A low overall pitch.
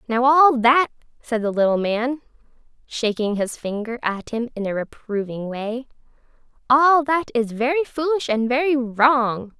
No: high, 245 Hz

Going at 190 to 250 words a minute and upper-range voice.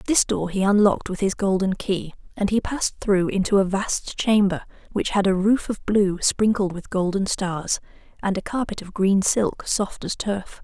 Yes: average, 200 wpm; high, 200 Hz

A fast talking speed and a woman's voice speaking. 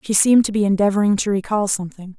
Yes: fast, 220 wpm; female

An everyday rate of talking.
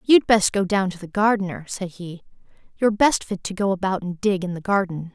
No: fast, 235 wpm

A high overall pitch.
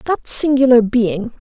Yes: high, 240 Hz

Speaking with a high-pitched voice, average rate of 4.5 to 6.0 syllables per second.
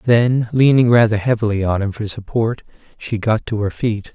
No: low, 110 Hz; 5.0 syllables/s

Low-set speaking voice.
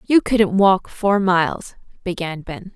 No: high, 190 Hz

